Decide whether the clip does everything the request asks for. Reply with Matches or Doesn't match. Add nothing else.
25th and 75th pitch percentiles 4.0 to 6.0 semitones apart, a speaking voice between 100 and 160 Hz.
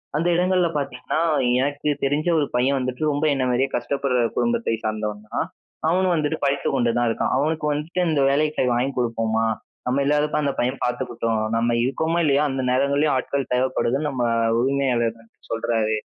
Doesn't match